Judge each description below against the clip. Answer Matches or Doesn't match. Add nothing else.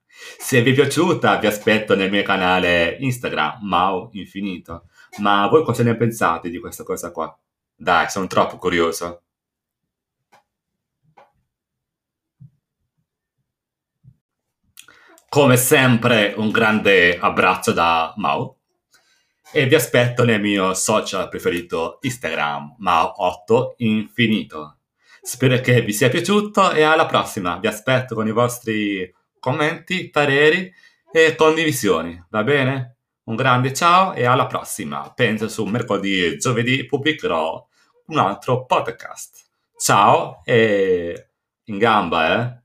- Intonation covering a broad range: Matches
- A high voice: Doesn't match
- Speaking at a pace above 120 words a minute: Doesn't match